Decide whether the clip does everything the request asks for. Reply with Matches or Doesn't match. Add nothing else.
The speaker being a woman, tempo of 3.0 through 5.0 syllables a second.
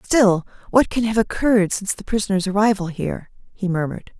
Doesn't match